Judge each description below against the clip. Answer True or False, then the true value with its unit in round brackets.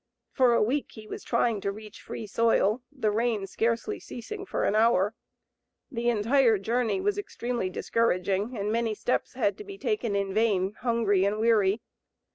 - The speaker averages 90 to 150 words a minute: False (170 wpm)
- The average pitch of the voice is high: True (225 Hz)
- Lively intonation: False (2.9 semitones)